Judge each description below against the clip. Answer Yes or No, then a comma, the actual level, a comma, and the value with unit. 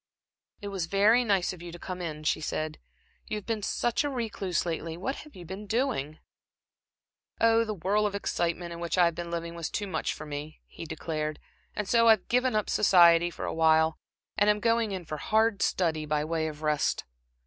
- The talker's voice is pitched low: No, medium, 180 Hz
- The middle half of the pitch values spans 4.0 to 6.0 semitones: Yes, average, 4.7 semitones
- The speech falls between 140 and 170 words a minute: No, fast, 205 wpm